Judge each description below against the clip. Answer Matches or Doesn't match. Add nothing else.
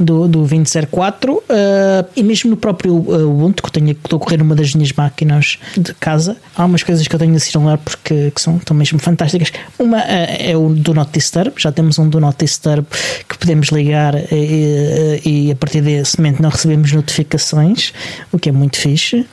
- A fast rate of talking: Matches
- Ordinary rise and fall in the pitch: Doesn't match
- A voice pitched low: Doesn't match